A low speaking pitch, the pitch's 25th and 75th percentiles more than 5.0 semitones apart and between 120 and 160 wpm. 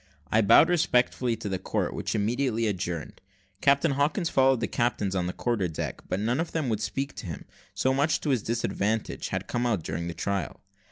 No: low, 115 Hz; wide, 5.5 semitones; fast, 205 wpm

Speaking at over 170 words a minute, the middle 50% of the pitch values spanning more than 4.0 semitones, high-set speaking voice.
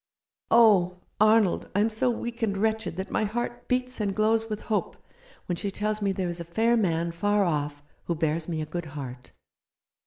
Yes: average, 195 wpm; average, 4.6 semitones; high, 200 Hz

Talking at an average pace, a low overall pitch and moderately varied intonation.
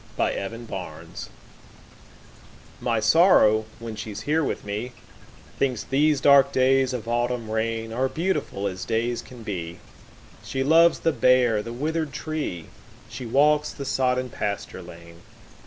No: slow, 125 wpm; low, 120 Hz; average, 4.1 semitones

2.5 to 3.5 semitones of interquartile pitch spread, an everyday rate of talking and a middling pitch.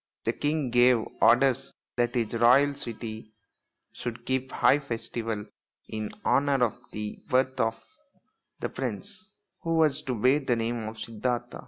No: average, 3.1 semitones; average, 145 wpm; low, 120 Hz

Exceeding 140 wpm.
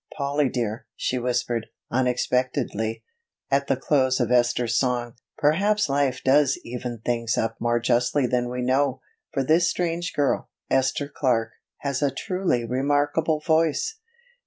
No: slow, 135 wpm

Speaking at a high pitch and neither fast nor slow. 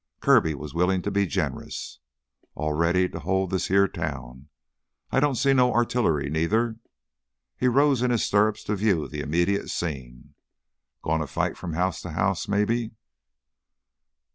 No: very low, 95 Hz; average, 155 wpm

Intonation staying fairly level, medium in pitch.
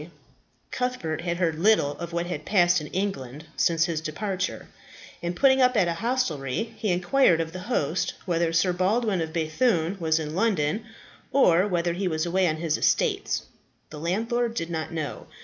No: average, 4.1 semitones; medium, 175 Hz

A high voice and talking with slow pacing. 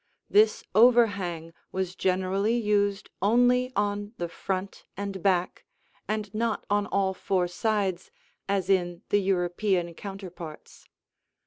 Yes: high, 195 Hz; slow, 115 wpm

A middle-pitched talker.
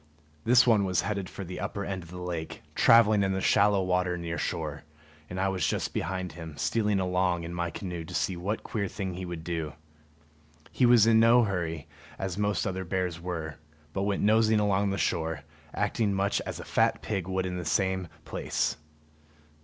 No: very low, 95 Hz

